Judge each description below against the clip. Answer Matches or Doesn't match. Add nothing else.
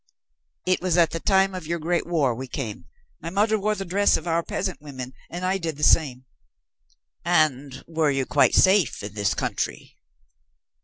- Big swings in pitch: Doesn't match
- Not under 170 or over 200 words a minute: Matches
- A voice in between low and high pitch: Matches